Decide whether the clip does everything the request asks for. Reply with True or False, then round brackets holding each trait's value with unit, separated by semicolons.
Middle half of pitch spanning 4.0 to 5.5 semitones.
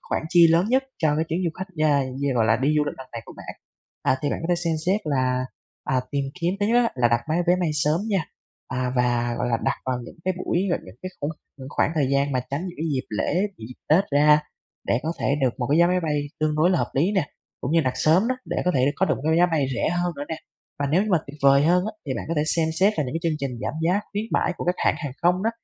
True (4.8 semitones)